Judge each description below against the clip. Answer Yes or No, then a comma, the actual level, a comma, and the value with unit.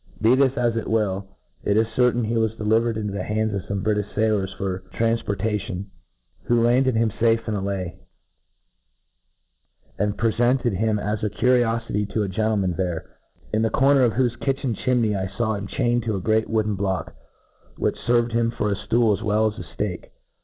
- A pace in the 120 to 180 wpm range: No, average, 195 wpm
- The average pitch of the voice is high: No, low, 110 Hz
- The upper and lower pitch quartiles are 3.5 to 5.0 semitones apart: No, narrow, 2.5 semitones